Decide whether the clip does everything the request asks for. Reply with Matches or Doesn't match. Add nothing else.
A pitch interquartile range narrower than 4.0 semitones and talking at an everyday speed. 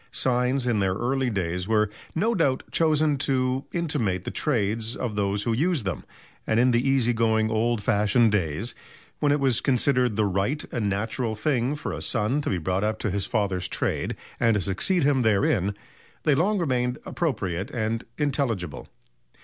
Doesn't match